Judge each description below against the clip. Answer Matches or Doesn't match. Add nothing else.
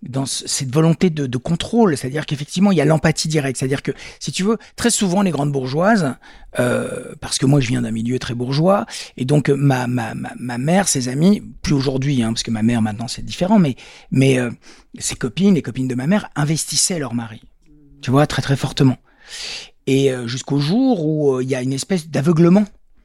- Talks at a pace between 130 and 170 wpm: Doesn't match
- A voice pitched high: Doesn't match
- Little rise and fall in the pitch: Doesn't match